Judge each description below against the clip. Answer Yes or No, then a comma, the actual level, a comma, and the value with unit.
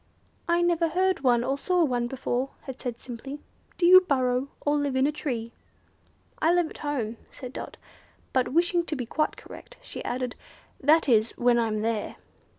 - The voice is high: Yes, very high, 270 Hz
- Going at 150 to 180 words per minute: No, average, 190 wpm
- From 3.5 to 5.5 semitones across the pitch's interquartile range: Yes, average, 5.1 semitones